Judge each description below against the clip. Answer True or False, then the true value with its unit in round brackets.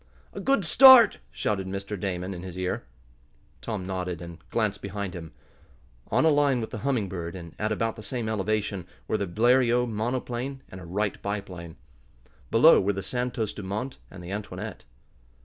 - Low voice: True (100 Hz)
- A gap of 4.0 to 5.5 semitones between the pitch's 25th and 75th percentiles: True (4.3 semitones)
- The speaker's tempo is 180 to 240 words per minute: False (170 wpm)